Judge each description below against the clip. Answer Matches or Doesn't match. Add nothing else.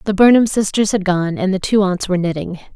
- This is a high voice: Matches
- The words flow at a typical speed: Doesn't match